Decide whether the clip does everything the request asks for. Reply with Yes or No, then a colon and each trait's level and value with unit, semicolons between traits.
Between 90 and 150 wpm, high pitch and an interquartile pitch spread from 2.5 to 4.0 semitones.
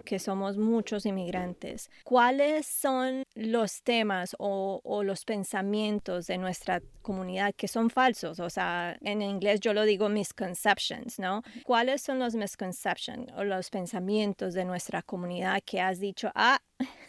Yes: average, 145 wpm; high, 205 Hz; average, 3.6 semitones